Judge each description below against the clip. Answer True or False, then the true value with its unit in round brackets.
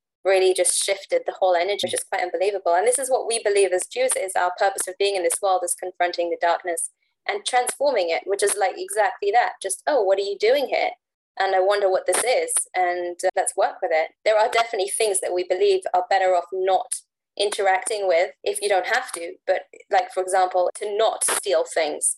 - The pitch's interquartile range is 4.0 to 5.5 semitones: True (5.0 semitones)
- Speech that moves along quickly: True (225 wpm)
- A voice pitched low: False (195 Hz)